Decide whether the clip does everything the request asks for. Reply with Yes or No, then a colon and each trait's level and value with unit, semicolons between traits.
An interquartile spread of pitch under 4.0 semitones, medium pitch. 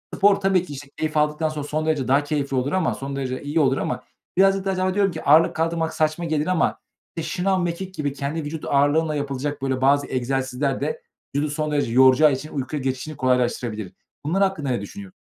Yes: average, 3.3 semitones; medium, 150 Hz